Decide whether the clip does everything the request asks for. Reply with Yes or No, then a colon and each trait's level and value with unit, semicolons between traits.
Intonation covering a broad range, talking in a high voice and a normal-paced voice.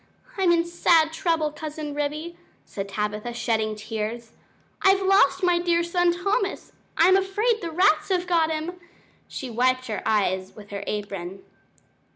Yes: wide, 8.3 semitones; very high, 315 Hz; average, 150 wpm